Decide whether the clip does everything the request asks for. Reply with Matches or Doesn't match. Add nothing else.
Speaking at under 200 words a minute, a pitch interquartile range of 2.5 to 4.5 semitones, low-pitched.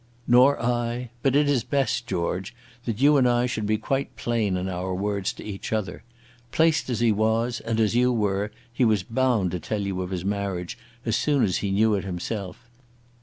Doesn't match